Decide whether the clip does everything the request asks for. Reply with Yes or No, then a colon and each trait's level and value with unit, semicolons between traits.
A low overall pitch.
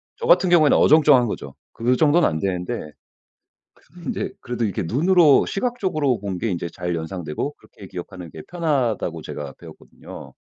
Yes: low, 120 Hz